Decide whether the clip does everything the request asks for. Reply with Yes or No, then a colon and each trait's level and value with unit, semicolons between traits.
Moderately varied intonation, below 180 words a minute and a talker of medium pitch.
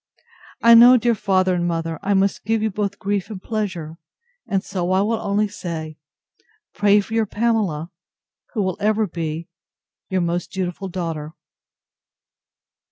No: average, 3.5 semitones; average, 150 wpm; high, 195 Hz